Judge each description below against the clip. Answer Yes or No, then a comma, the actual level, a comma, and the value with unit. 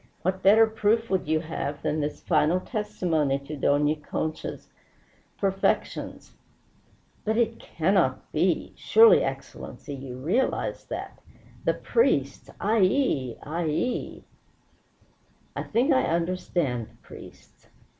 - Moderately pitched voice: Yes, medium, 175 Hz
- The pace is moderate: No, slow, 115 wpm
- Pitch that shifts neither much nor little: No, wide, 6.4 semitones